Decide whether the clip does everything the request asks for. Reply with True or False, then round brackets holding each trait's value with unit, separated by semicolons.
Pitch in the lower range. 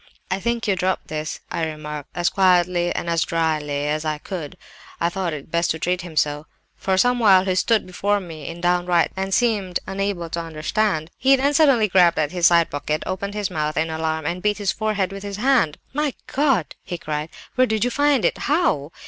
False (180 Hz)